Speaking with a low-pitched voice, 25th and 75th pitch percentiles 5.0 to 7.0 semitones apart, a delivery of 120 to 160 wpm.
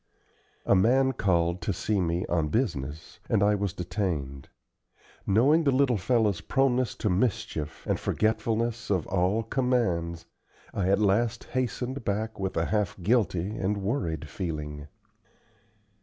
Yes: low, 100 Hz; wide, 5.4 semitones; slow, 135 wpm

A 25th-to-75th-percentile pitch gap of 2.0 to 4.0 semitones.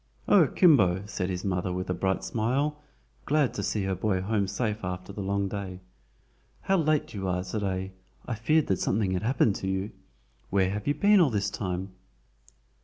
Yes: average, 3.6 semitones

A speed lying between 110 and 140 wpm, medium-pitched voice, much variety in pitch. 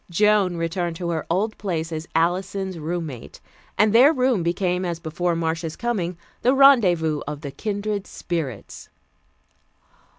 No: slow, 135 wpm; medium, 175 Hz; average, 3.9 semitones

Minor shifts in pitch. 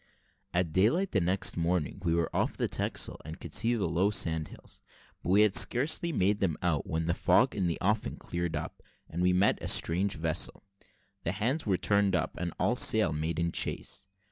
No: average, 3.7 semitones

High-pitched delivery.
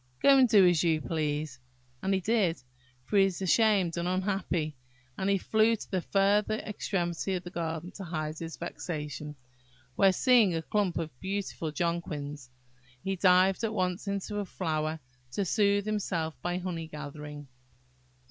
No: medium, 180 Hz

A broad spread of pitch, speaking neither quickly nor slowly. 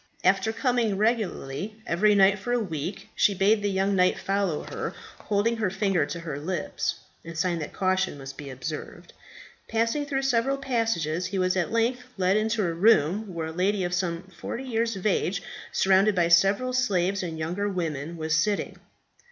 No: average, 4.3 semitones; average, 180 wpm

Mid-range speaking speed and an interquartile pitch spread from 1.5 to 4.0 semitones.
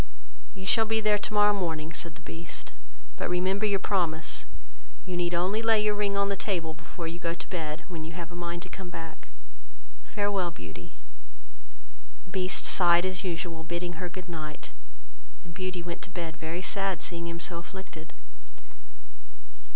Yes: average, 175 wpm; narrow, 2.6 semitones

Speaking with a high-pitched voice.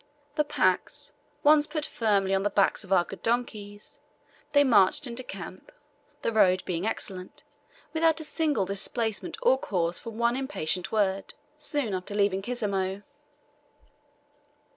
Yes: high, 215 Hz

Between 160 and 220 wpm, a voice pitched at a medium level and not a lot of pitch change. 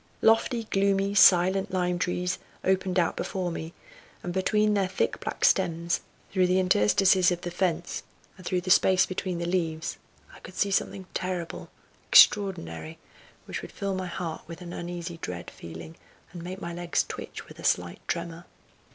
Yes: average, 170 wpm; medium, 180 Hz; narrow, 1.9 semitones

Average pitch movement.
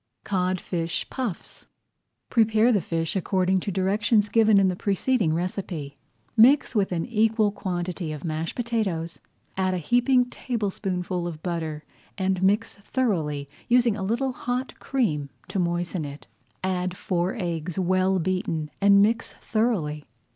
Yes: average, 4.2 semitones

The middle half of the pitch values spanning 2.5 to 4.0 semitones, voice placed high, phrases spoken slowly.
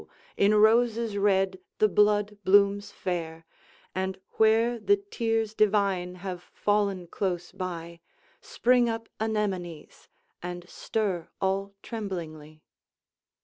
Yes: average, 3.2 semitones; high, 200 Hz; slow, 105 wpm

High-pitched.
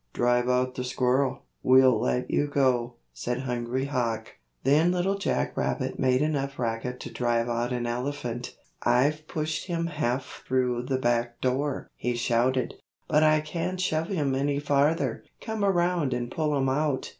No: low, 130 Hz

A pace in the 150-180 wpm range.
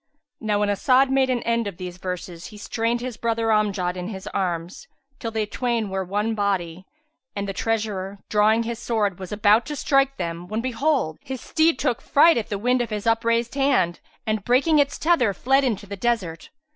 No: average, 195 wpm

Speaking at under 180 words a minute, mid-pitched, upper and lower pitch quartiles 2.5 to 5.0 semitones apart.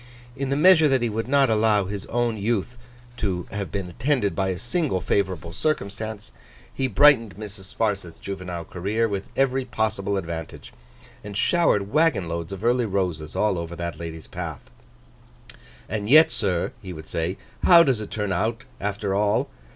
No: average, 165 wpm; low, 105 Hz; average, 4.3 semitones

